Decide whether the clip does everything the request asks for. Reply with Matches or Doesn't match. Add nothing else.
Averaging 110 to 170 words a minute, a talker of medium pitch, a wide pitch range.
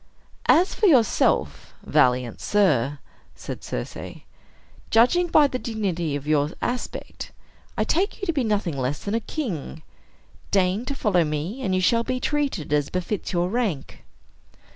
Doesn't match